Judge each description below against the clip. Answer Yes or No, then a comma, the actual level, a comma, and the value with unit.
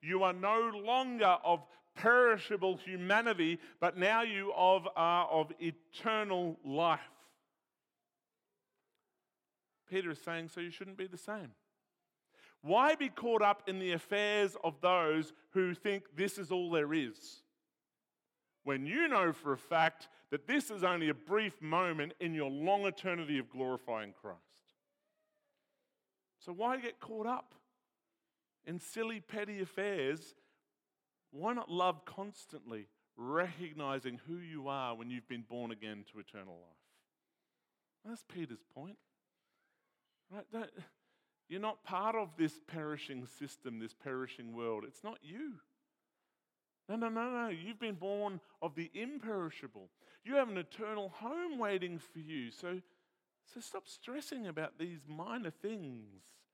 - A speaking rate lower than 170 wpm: Yes, slow, 135 wpm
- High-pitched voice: No, medium, 180 Hz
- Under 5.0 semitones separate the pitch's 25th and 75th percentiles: No, wide, 5.5 semitones